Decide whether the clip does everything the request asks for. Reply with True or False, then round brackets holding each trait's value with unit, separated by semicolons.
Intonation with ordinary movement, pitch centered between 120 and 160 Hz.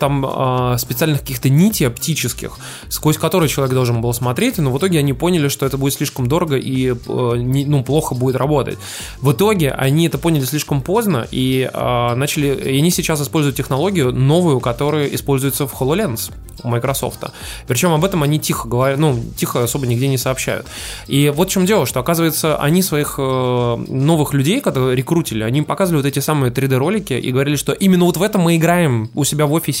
True (3.7 semitones; 140 Hz)